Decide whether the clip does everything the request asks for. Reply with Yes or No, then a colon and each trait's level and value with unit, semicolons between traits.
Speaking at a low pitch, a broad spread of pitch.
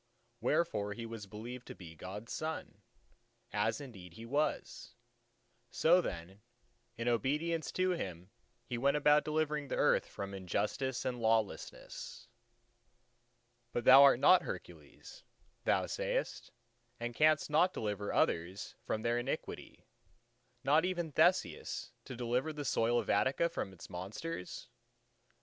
Yes: low, 120 Hz; wide, 6.3 semitones